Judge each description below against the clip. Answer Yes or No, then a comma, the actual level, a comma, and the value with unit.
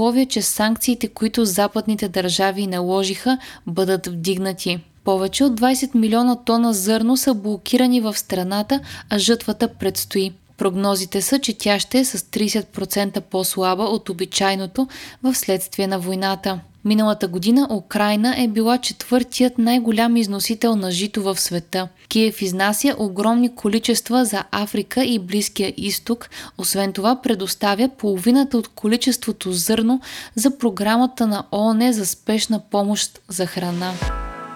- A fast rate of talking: No, average, 125 wpm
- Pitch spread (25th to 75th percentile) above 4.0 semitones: No, average, 3.3 semitones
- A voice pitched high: Yes, high, 215 Hz